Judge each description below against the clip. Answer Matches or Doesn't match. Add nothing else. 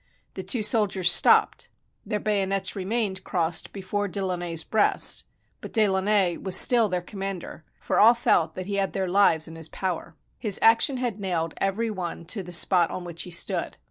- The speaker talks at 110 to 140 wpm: Doesn't match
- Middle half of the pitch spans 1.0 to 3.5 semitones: Matches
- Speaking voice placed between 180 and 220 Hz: Matches